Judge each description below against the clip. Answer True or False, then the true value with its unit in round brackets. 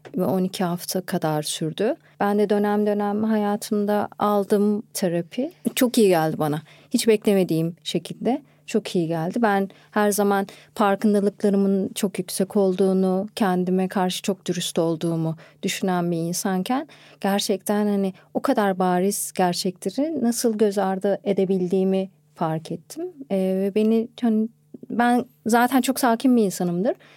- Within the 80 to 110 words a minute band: False (125 wpm)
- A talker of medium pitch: False (200 Hz)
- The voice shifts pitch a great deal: False (2.9 semitones)